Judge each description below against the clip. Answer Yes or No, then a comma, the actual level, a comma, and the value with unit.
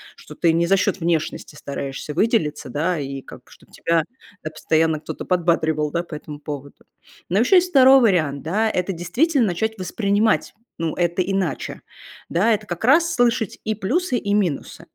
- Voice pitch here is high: No, medium, 180 Hz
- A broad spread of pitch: Yes, wide, 5.8 semitones